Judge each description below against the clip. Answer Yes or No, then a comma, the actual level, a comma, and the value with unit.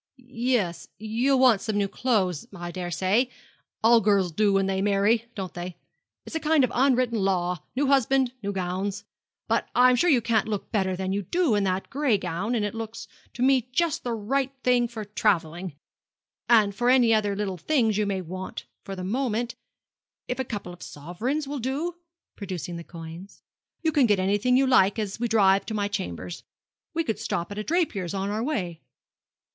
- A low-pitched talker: No, high, 210 Hz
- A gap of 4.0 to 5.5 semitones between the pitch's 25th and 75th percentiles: Yes, average, 4.7 semitones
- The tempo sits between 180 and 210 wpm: Yes, average, 190 wpm